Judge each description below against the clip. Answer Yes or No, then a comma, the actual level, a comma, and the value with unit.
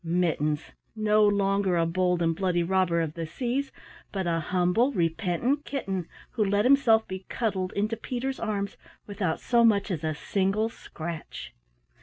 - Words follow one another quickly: No, average, 155 wpm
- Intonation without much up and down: No, average, 4.2 semitones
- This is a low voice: No, high, 190 Hz